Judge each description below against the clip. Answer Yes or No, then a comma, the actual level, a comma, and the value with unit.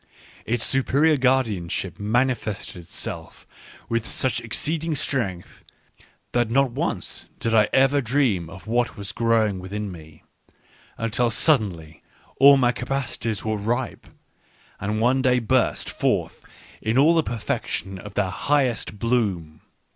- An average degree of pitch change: Yes, average, 4.3 semitones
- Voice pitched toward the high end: No, low, 115 Hz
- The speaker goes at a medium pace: No, slow, 130 wpm